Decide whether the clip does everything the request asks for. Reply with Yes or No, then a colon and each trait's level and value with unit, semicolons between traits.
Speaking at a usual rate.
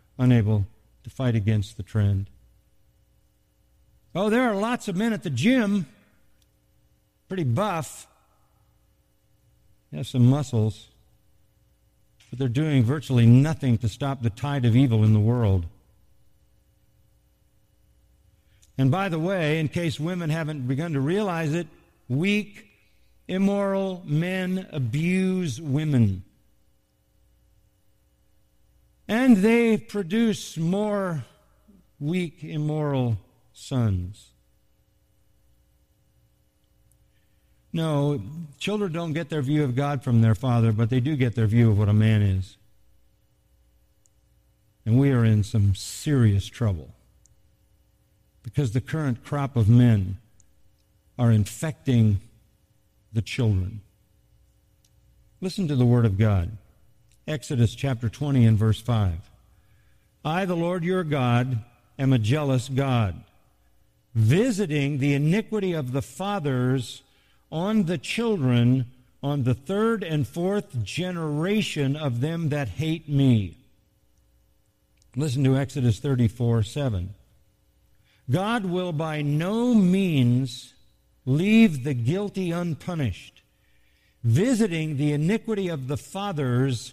No: slow, 110 wpm